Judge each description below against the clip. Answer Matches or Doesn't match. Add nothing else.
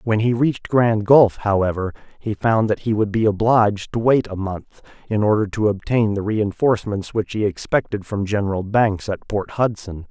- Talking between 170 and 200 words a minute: Matches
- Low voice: Matches